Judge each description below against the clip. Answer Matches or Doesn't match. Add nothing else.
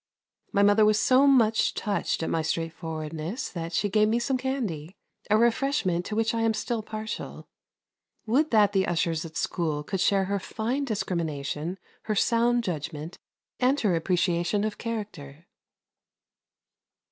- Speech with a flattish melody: Doesn't match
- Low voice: Doesn't match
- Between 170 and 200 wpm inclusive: Doesn't match